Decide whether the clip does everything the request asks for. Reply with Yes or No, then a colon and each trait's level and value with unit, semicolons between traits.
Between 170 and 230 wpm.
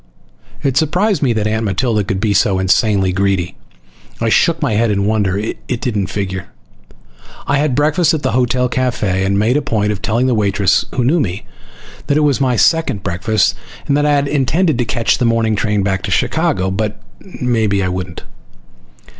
Yes: average, 190 wpm